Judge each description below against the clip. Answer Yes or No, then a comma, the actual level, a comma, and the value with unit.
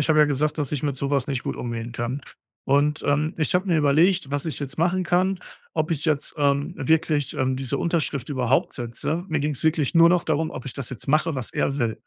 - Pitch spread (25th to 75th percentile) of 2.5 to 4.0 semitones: Yes, average, 2.9 semitones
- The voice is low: No, medium, 145 Hz